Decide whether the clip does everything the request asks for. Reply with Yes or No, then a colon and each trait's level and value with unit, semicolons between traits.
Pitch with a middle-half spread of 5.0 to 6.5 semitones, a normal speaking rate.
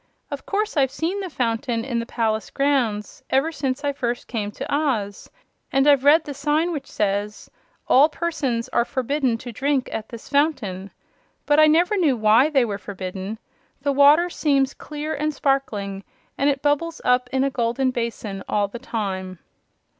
No: average, 4.6 semitones; average, 175 wpm